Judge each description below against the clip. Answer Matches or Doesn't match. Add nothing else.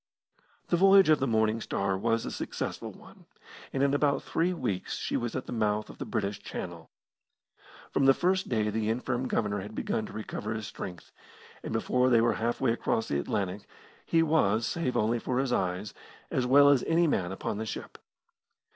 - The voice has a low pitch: Matches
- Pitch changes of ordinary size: Matches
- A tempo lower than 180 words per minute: Doesn't match